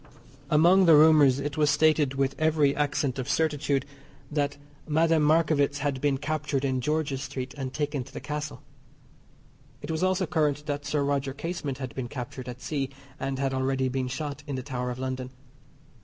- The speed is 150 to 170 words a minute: No, average, 180 wpm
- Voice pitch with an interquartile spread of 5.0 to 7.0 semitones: No, narrow, 2.4 semitones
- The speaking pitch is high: No, medium, 145 Hz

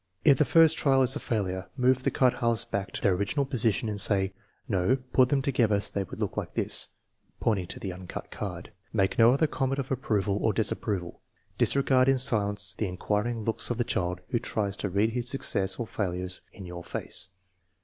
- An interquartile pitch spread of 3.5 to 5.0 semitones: Yes, average, 4.7 semitones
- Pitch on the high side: No, low, 110 Hz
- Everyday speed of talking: No, fast, 215 wpm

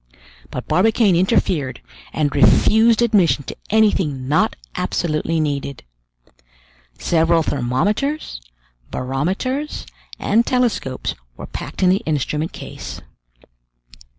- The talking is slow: Yes, slow, 95 wpm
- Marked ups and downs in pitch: Yes, wide, 7.4 semitones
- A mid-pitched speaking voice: Yes, medium, 170 Hz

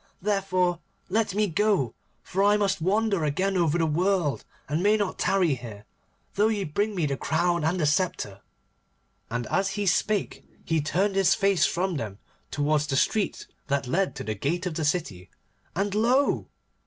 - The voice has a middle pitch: Yes, medium, 180 Hz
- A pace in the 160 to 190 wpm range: Yes, average, 175 wpm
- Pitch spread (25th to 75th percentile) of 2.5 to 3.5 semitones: No, average, 4.9 semitones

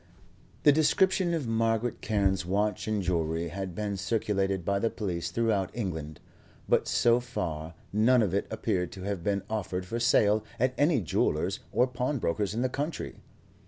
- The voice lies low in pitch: Yes, low, 105 Hz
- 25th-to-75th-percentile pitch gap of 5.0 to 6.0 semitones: No, average, 4.4 semitones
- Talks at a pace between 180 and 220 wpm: No, average, 160 wpm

